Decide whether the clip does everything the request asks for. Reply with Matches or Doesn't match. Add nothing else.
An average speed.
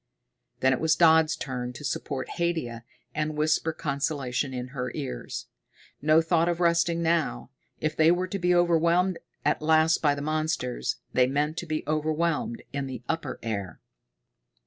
Matches